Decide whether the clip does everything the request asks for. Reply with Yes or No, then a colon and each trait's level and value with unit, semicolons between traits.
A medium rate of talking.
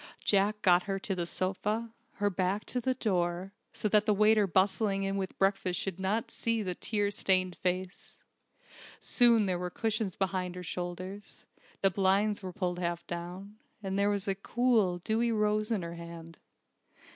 Yes: average, 170 wpm